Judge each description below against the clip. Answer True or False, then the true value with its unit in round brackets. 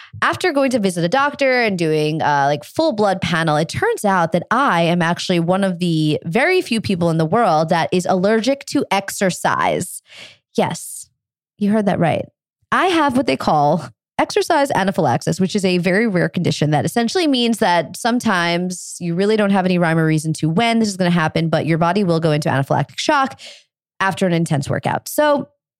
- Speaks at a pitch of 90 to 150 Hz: False (185 Hz)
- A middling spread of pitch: False (5.9 semitones)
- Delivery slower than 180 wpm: False (200 wpm)